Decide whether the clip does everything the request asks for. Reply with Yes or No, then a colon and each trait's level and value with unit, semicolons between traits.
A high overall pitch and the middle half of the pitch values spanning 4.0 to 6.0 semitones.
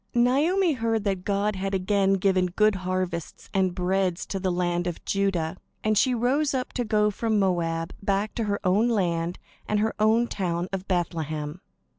No: high, 195 Hz; average, 3.2 semitones